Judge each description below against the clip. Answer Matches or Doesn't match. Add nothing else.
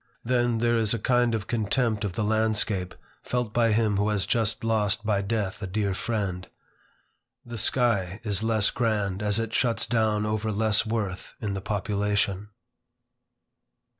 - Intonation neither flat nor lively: Doesn't match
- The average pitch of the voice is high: Doesn't match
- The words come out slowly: Doesn't match